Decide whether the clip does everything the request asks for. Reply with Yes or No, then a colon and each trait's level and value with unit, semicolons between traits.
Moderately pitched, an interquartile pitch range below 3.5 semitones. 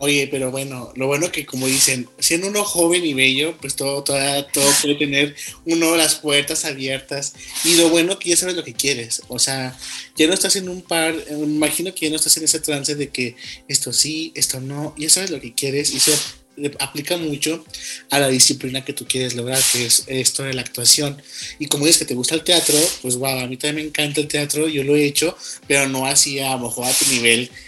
Yes: medium, 145 Hz; average, 2.9 semitones